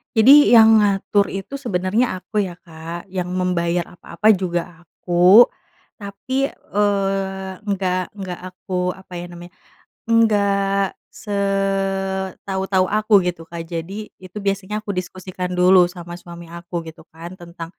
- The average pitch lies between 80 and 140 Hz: No, high, 190 Hz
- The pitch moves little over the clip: Yes, narrow, 2.2 semitones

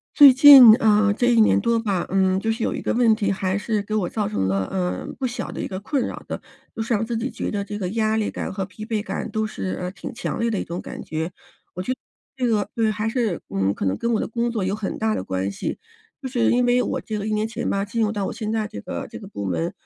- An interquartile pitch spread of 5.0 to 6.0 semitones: No, average, 3.3 semitones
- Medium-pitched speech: No, high, 215 Hz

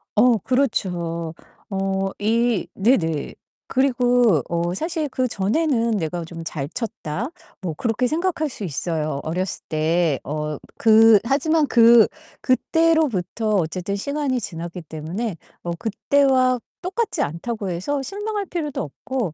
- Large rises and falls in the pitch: Yes, wide, 7.4 semitones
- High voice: Yes, high, 220 Hz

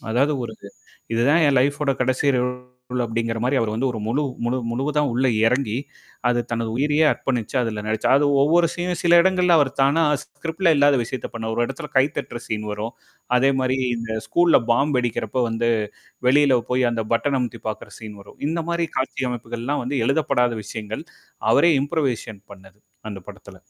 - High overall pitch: No, low, 125 Hz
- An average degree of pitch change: Yes, average, 3.9 semitones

